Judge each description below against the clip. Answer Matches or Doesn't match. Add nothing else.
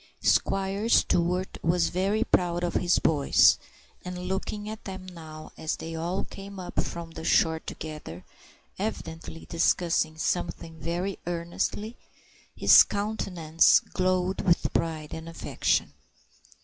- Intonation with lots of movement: Doesn't match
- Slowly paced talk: Matches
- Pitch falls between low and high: Matches